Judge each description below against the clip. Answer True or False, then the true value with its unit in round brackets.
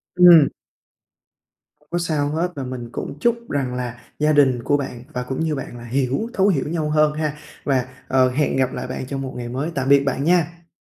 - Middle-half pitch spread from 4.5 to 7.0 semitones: False (3.6 semitones)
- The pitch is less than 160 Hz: True (140 Hz)